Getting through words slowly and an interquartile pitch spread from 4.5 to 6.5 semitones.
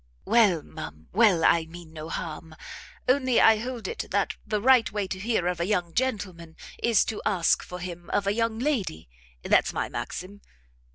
No: average, 180 wpm; average, 5.1 semitones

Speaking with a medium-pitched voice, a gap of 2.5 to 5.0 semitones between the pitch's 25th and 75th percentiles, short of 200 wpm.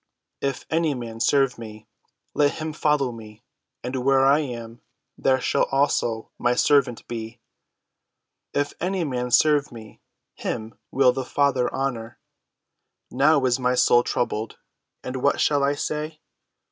No: low, 130 Hz; average, 3.2 semitones; average, 140 wpm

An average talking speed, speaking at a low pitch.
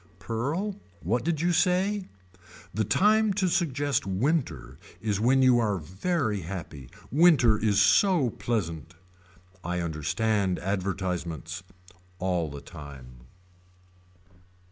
No: slow, 105 wpm; low, 105 Hz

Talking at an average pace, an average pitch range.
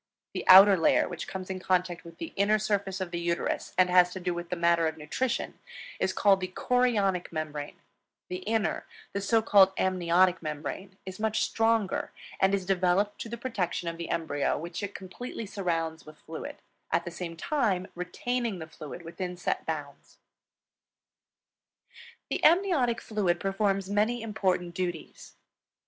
Yes: average, 165 wpm; average, 3.2 semitones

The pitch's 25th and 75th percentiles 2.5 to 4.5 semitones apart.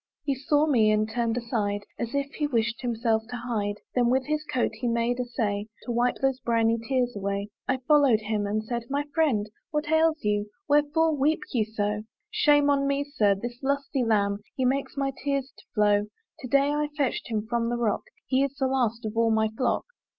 Yes: average, 4.1 semitones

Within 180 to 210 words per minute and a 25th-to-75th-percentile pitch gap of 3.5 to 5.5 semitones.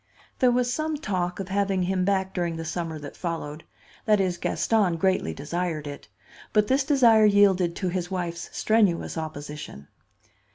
No: average, 160 wpm; average, 3.8 semitones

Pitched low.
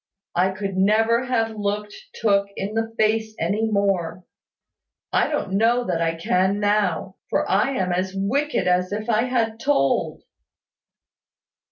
No: high, 205 Hz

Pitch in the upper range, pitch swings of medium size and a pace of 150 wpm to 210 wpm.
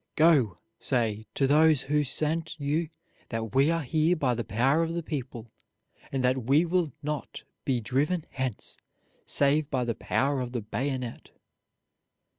No: medium, 140 Hz; average, 3.9 semitones; average, 155 wpm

